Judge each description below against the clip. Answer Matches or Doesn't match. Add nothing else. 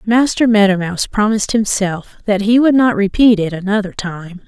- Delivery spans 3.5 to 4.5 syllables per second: Doesn't match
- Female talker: Matches